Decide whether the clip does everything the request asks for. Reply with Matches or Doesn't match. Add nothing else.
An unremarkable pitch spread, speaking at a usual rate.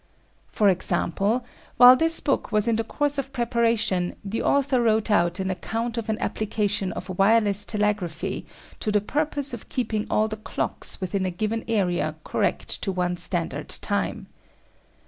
Matches